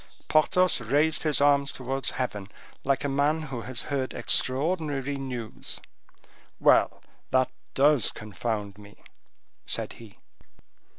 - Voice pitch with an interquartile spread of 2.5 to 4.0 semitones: Yes, average, 3.3 semitones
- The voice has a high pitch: No, low, 135 Hz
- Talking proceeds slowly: Yes, slow, 115 wpm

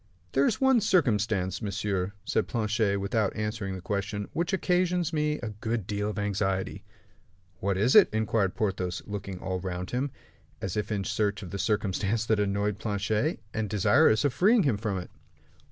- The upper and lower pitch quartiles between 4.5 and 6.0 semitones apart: No, average, 2.9 semitones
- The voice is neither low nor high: No, low, 105 Hz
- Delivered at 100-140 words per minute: No, average, 170 wpm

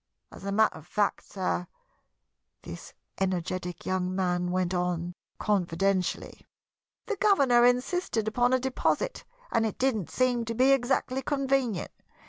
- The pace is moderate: No, slow, 130 wpm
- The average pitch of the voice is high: Yes, high, 215 Hz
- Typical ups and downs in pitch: No, wide, 5.8 semitones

